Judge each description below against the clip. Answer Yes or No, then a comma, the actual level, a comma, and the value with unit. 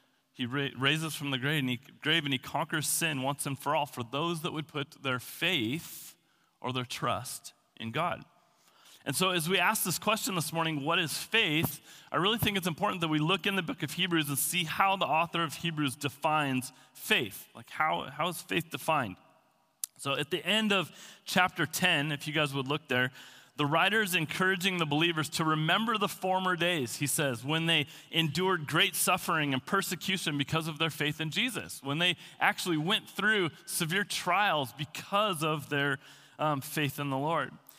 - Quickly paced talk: No, average, 195 wpm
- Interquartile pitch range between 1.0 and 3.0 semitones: No, average, 4.1 semitones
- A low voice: No, medium, 160 Hz